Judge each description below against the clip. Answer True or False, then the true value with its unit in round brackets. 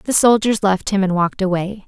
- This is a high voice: True (200 Hz)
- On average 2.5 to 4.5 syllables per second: False (5.5 syllables/s)